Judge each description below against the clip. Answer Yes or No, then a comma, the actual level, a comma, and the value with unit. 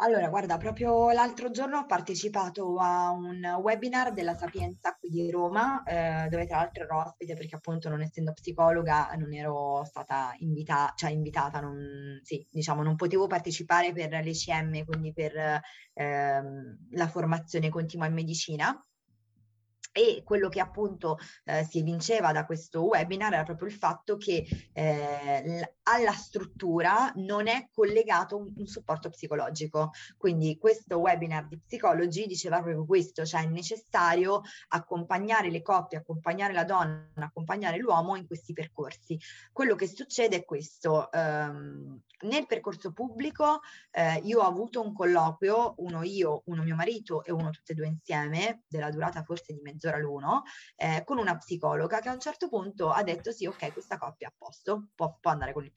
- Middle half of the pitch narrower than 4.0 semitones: No, average, 4.4 semitones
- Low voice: No, medium, 170 Hz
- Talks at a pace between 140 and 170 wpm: Yes, average, 160 wpm